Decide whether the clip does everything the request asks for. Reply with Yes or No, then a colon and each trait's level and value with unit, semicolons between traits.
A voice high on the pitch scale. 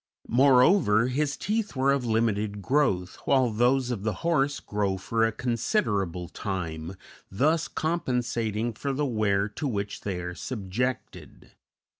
No: low, 115 Hz